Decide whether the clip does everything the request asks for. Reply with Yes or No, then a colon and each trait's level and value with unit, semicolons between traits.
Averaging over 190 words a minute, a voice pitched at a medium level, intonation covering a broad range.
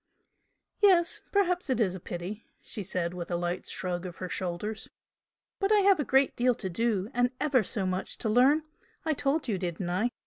No: average, 200 wpm; high, 215 Hz; wide, 7.3 semitones